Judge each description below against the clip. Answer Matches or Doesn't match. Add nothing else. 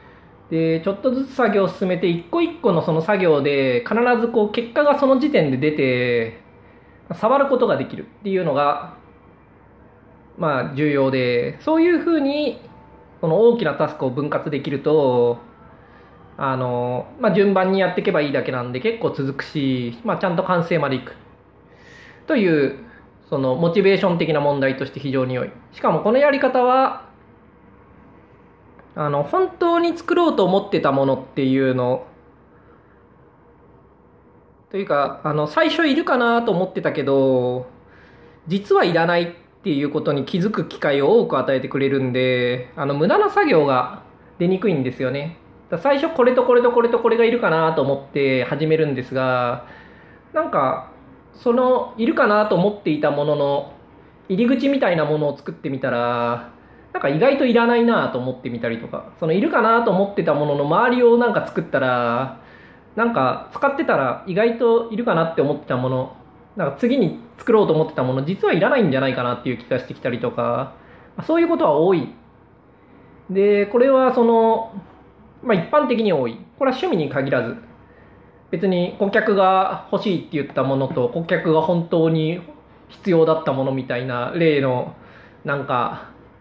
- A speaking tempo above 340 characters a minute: Doesn't match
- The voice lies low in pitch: Doesn't match